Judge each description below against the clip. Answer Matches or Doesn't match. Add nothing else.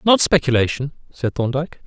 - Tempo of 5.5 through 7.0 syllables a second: Matches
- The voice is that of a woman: Doesn't match